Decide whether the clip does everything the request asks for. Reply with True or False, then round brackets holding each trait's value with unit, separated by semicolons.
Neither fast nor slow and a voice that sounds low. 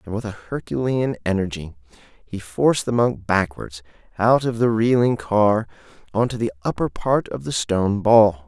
True (170 wpm; 105 Hz)